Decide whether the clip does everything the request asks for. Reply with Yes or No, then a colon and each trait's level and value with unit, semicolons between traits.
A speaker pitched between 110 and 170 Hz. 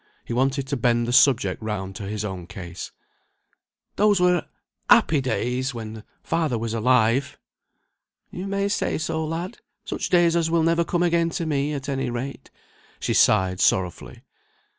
Yes: low, 135 Hz